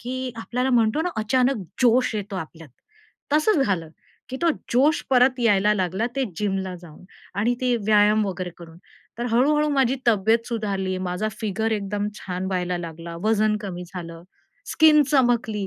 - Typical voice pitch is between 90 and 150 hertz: No, high, 215 Hz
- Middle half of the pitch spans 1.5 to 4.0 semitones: No, average, 4.9 semitones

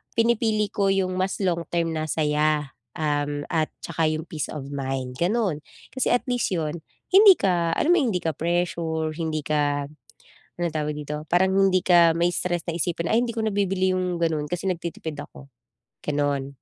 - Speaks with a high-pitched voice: No, medium, 170 Hz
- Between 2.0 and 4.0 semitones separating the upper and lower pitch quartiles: Yes, average, 3.7 semitones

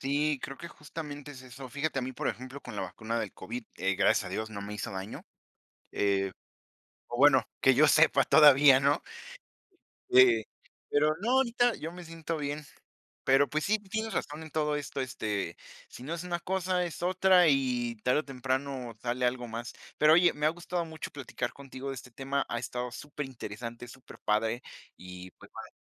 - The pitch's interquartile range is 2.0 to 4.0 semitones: No, average, 4.4 semitones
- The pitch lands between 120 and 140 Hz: Yes, low, 135 Hz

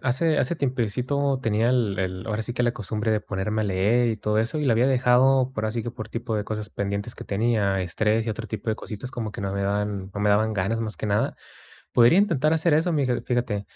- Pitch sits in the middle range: No, low, 110 Hz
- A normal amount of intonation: Yes, average, 3.2 semitones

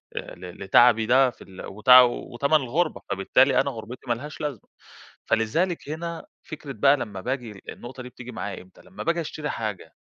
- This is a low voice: Yes, low, 125 Hz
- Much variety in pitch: No, average, 4.5 semitones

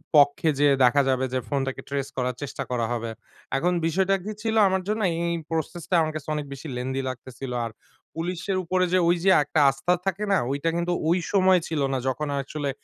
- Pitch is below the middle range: No, medium, 155 Hz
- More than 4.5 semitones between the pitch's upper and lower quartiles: Yes, average, 5.0 semitones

